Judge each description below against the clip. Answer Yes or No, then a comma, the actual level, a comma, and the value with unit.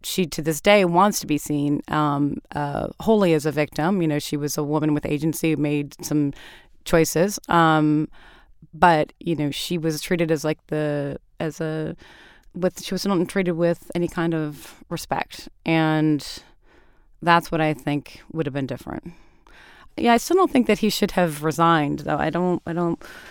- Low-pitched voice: No, medium, 160 Hz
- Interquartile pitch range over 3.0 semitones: No, narrow, 2.6 semitones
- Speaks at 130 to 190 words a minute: Yes, average, 185 wpm